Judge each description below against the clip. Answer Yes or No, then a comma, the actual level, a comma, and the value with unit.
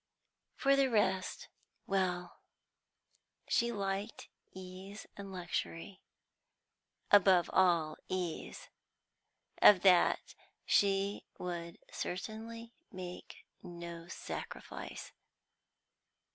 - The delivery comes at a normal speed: No, slow, 75 wpm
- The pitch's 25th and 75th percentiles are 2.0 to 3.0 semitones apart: Yes, narrow, 2.4 semitones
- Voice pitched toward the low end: No, high, 190 Hz